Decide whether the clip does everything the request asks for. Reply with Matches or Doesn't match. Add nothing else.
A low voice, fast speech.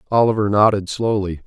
Doesn't match